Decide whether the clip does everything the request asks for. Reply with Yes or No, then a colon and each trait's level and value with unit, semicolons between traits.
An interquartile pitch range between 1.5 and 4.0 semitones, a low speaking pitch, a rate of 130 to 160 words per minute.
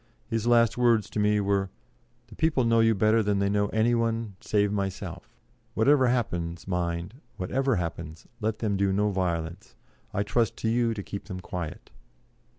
No: average, 3.3 semitones; low, 105 Hz; average, 170 wpm